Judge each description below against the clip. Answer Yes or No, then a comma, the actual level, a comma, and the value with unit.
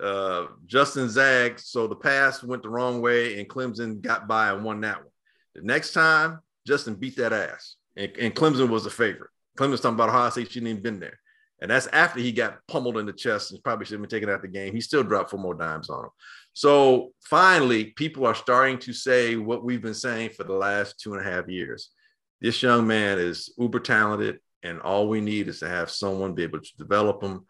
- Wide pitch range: No, average, 3.7 semitones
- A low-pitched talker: Yes, low, 115 Hz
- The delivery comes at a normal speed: No, fast, 230 wpm